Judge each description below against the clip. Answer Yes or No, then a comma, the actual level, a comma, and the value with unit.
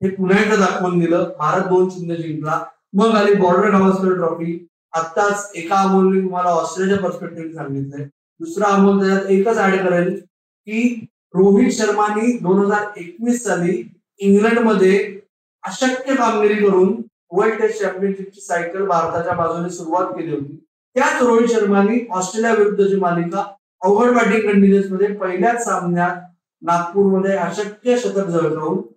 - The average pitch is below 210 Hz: Yes, high, 190 Hz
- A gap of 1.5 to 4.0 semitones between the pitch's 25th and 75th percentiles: Yes, average, 2.9 semitones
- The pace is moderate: Yes, average, 110 wpm